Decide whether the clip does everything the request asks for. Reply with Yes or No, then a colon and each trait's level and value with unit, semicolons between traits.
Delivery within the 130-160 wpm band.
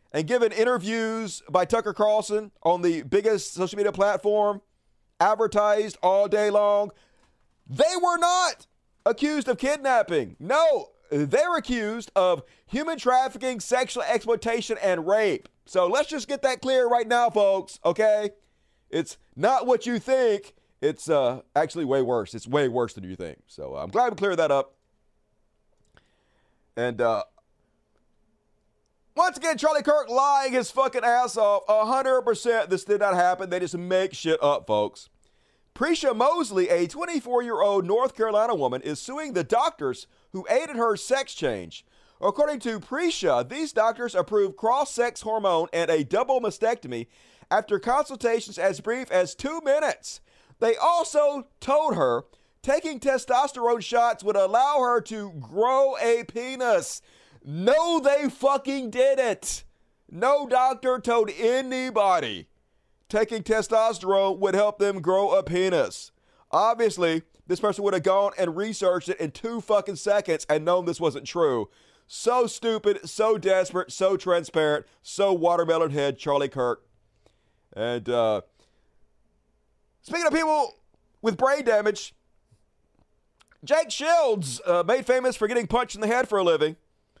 Yes: average, 140 wpm